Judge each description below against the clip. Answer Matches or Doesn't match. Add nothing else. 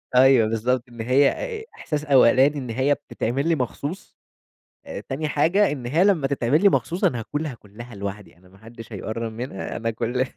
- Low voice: Matches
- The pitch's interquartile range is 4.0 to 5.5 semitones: Matches